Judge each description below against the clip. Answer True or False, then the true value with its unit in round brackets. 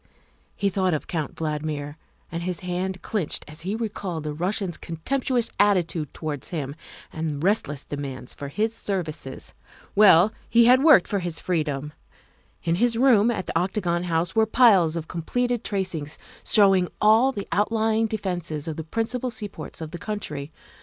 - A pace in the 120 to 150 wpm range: False (160 wpm)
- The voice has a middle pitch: True (180 Hz)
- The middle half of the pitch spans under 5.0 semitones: False (5.4 semitones)